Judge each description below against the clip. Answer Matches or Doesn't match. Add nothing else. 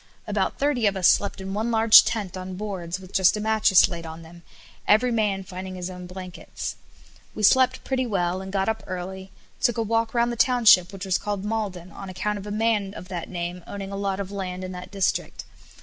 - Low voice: Doesn't match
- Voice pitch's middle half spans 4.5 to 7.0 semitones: Doesn't match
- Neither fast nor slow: Doesn't match